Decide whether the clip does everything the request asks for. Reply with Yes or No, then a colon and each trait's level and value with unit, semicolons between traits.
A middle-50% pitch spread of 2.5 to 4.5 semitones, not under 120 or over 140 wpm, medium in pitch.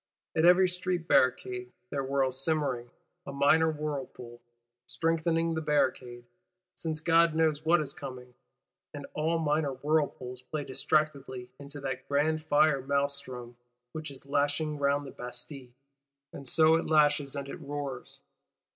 Yes: average, 3.3 semitones; slow, 135 wpm; medium, 145 Hz